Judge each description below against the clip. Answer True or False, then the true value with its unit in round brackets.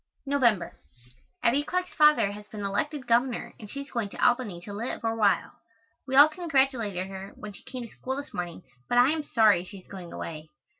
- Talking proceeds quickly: True (210 wpm)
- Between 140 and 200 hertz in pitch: False (230 Hz)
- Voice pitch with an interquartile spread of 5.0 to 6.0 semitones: True (5.4 semitones)